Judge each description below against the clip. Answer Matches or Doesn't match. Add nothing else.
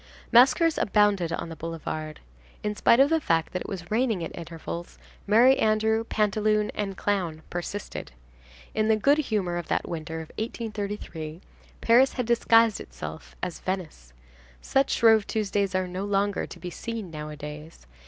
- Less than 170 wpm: Matches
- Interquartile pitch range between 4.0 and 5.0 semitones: Matches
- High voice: Matches